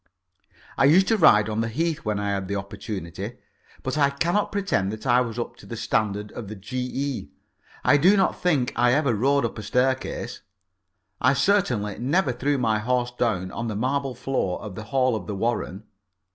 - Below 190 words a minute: No, average, 195 wpm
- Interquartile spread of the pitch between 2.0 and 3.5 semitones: No, average, 4.8 semitones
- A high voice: No, low, 120 Hz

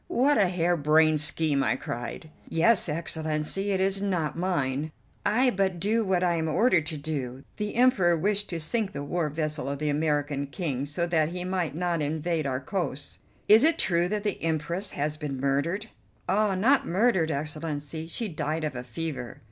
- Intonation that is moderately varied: Yes, average, 4.2 semitones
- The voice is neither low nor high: Yes, medium, 165 Hz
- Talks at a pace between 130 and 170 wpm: No, average, 180 wpm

